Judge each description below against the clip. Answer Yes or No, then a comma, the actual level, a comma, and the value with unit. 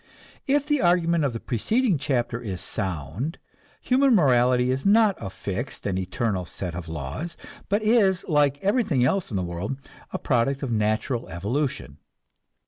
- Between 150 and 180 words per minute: Yes, average, 155 wpm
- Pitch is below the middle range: Yes, low, 130 Hz